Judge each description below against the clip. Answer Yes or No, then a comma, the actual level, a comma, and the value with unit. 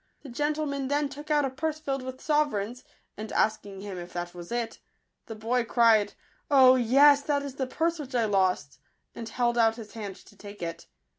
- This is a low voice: No, high, 245 Hz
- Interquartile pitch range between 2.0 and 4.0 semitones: No, average, 5.3 semitones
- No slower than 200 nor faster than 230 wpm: Yes, fast, 205 wpm